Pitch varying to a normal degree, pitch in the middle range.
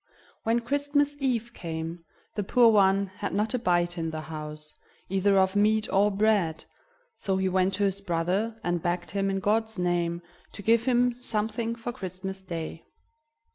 No: average, 4.2 semitones; high, 195 Hz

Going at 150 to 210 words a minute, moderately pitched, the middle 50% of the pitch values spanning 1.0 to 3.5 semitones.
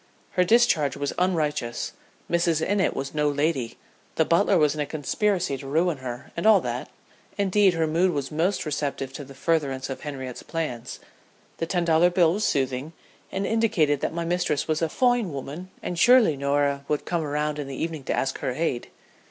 No: average, 190 wpm; medium, 155 Hz; average, 4.1 semitones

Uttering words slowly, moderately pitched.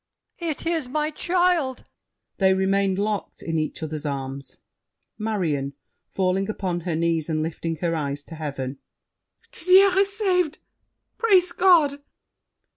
No: slow, 125 wpm; high, 195 Hz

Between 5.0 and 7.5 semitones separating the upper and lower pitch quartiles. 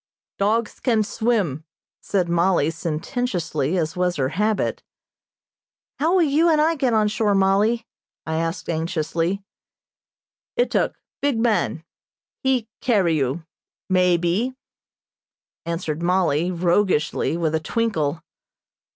Yes: wide, 5.6 semitones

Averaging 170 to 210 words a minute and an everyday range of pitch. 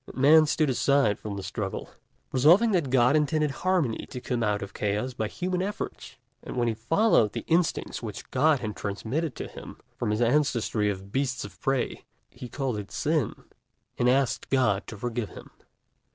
No: average, 180 wpm; wide, 5.7 semitones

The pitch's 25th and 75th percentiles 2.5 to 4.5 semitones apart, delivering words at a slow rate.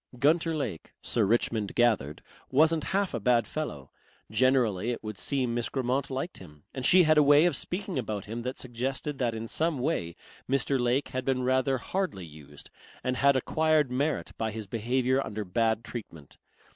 No: average, 4.2 semitones; average, 180 wpm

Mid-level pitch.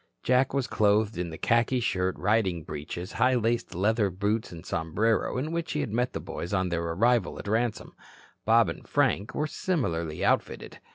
No: low, 105 Hz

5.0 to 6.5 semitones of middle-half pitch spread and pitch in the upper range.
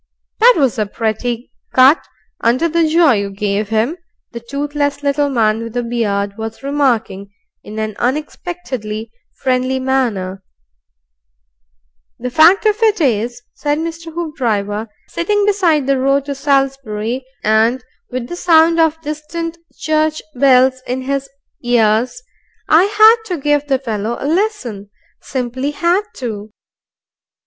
Yes: wide, 5.6 semitones; very high, 265 Hz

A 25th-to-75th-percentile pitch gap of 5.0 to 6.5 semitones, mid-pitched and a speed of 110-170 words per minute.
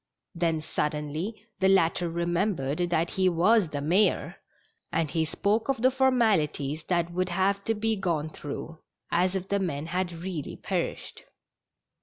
No: average, 3.7 semitones; medium, 175 Hz; average, 150 wpm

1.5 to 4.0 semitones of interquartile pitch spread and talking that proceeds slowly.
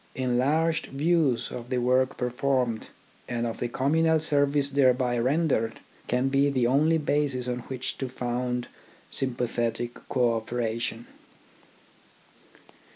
Yes: narrow, 2.6 semitones; slow, 115 wpm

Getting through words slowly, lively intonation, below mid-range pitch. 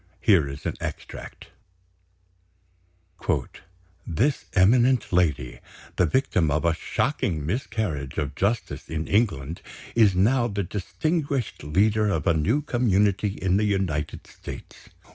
Yes: slow, 120 wpm; wide, 6.0 semitones; very low, 95 Hz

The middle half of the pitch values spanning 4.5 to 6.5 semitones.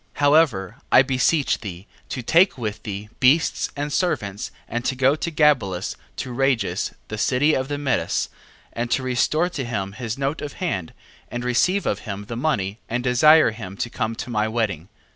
Yes: average, 5.1 semitones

